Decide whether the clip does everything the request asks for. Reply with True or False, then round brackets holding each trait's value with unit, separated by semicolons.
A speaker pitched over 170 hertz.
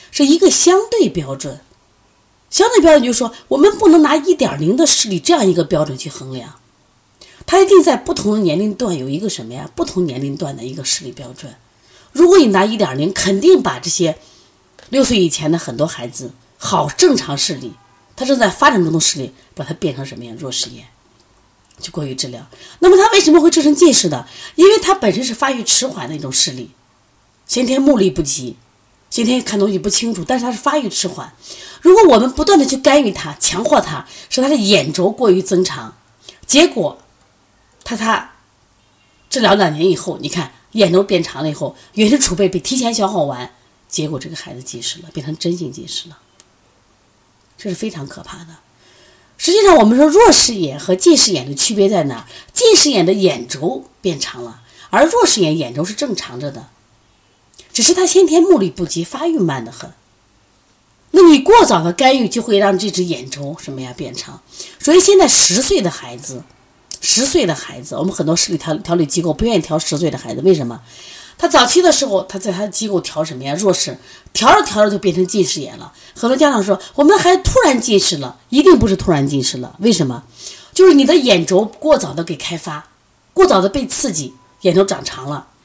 True (185 Hz)